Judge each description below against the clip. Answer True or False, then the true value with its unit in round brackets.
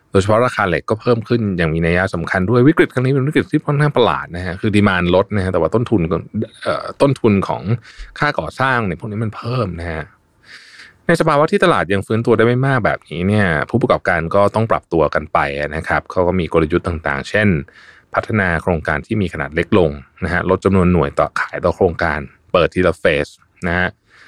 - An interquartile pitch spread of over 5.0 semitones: True (5.4 semitones)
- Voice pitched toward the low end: True (100 Hz)